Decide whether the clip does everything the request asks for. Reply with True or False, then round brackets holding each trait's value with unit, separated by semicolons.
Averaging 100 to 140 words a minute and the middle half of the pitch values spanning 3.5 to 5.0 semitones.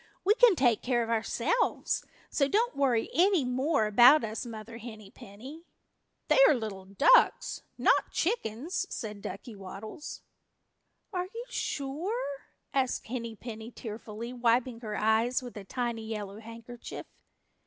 True (135 wpm; 4.5 semitones)